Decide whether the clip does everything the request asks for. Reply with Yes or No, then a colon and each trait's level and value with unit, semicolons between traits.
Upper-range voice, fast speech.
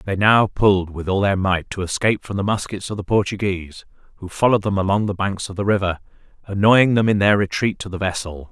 No: low, 100 Hz; fast, 225 wpm